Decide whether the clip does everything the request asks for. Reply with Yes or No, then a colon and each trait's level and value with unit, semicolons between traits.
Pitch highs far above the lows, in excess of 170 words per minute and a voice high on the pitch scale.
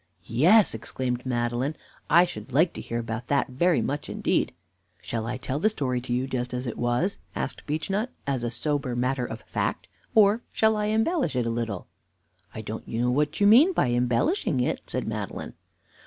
No: wide, 6.6 semitones; average, 185 wpm; low, 130 Hz